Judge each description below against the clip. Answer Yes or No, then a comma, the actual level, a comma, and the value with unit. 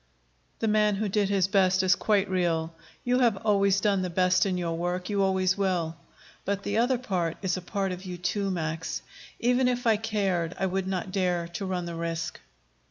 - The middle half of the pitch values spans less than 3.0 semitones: Yes, narrow, 2.4 semitones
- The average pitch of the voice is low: No, high, 190 Hz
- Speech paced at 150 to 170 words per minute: No, average, 200 wpm